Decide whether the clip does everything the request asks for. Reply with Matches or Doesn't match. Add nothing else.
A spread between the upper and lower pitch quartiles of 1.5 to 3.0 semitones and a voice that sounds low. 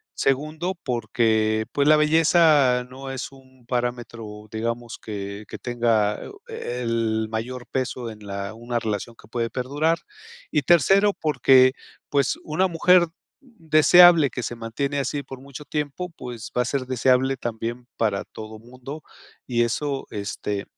Doesn't match